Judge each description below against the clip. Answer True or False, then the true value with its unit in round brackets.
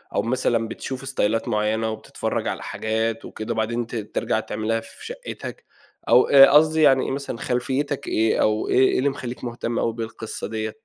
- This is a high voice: False (115 Hz)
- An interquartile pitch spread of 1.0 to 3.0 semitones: True (2.6 semitones)